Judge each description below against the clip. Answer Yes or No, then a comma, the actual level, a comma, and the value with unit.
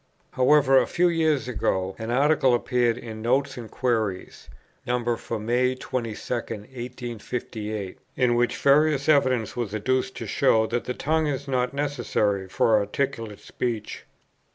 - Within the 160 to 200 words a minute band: No, average, 140 wpm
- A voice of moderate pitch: No, low, 120 Hz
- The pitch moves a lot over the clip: No, average, 3.3 semitones